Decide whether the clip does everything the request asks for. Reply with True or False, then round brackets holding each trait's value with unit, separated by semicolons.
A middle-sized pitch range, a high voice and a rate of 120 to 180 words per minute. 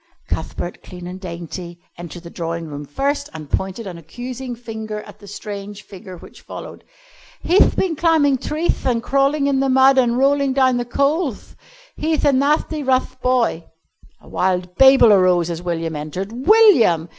False (7.3 semitones; 230 Hz; 165 wpm)